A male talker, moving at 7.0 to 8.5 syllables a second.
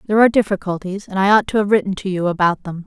No: female; 7.4 syllables/s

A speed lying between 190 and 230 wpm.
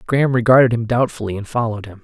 Yes: fast, 205 wpm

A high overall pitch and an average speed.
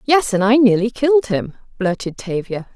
Yes: high, 220 Hz; average, 175 wpm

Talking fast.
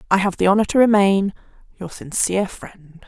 No: average, 175 wpm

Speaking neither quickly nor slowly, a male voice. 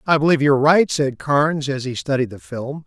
No: fast, 230 wpm; male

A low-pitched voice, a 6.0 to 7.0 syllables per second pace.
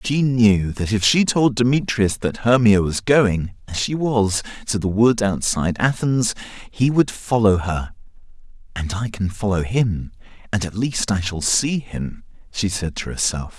No: low, 110 Hz; 4.2 syllables/s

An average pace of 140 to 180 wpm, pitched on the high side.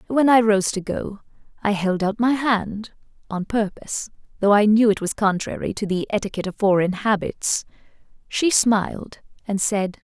Yes: average, 165 wpm; high, 210 Hz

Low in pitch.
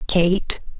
No: medium, 180 Hz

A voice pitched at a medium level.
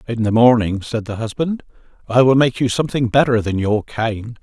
No: low, 115 Hz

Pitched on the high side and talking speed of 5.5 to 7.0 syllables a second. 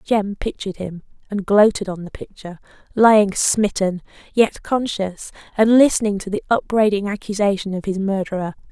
No: high, 200 Hz; 4.6 syllables/s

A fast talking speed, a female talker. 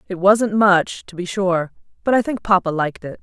Yes: fast, 225 wpm; female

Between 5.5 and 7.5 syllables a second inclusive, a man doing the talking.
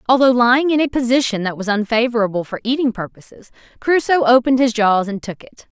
No: 6.1 syllables/s; female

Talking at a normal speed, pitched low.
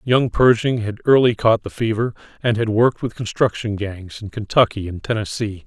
Yes: average, 180 wpm; low, 110 Hz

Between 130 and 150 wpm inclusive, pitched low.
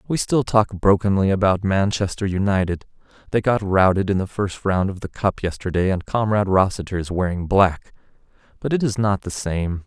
No: average, 170 wpm; low, 100 Hz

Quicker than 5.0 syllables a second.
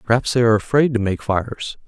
Yes: 6.5 syllables/s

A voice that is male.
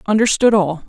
No: female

